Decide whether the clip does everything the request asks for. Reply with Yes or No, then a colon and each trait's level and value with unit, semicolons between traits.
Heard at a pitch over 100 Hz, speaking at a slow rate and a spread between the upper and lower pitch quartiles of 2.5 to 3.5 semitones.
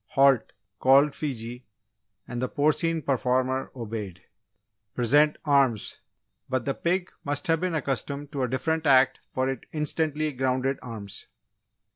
Yes: low, 135 Hz; slow, 130 wpm; average, 3.0 semitones